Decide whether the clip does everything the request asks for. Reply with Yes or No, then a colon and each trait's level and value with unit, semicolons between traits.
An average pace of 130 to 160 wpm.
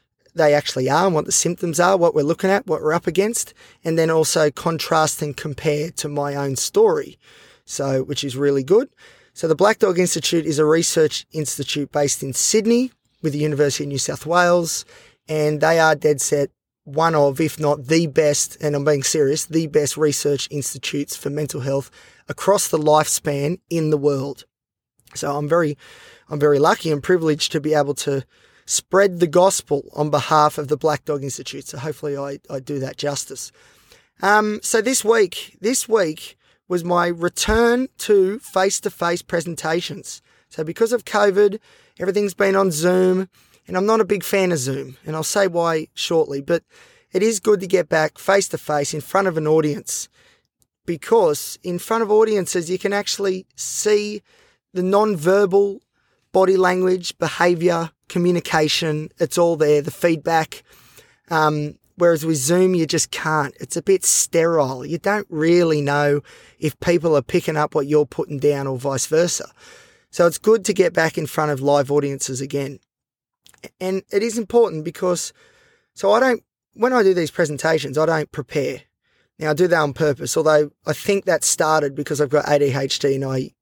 No: average, 180 wpm